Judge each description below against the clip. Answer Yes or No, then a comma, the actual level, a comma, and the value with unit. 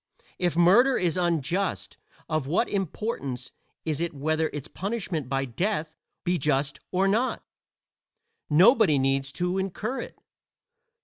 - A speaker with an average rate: No, slow, 125 wpm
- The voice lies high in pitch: No, medium, 170 Hz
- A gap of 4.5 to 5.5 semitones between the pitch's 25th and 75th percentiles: Yes, average, 4.8 semitones